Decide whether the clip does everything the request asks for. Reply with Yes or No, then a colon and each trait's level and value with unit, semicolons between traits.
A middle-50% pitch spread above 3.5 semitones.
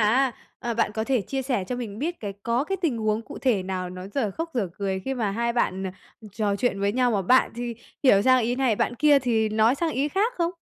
Yes: average, 4.3 semitones